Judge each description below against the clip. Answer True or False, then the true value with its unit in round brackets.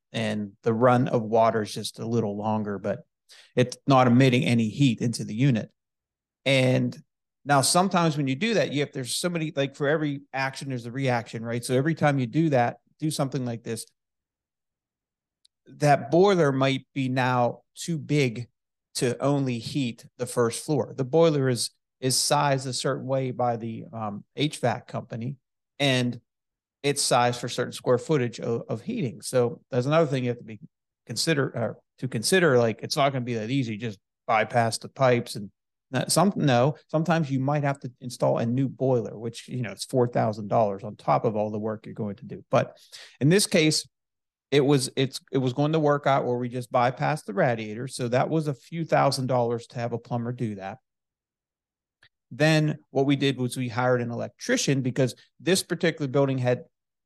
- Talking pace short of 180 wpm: False (190 wpm)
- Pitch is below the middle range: True (130 Hz)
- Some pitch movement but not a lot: True (3.5 semitones)